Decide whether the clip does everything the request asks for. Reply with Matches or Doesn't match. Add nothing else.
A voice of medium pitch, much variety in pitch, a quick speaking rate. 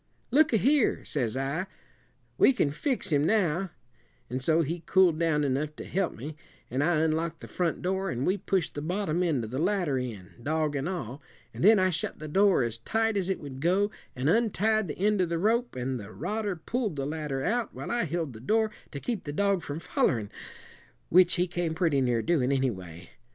Matches